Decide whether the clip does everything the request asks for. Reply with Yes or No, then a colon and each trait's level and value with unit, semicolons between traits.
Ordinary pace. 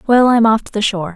No: fast, 310 wpm